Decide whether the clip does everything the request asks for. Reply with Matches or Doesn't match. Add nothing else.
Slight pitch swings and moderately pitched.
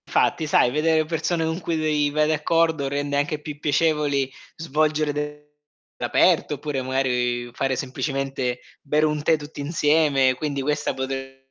Matches